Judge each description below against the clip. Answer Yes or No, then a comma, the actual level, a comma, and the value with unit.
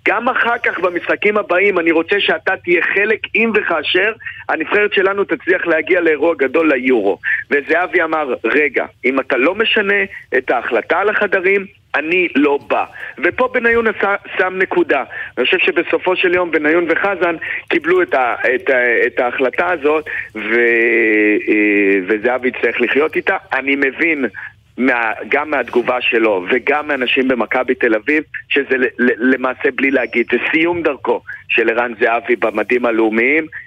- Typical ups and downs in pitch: No, wide, 8.0 semitones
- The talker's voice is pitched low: No, medium, 165 Hz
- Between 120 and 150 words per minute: Yes, average, 145 wpm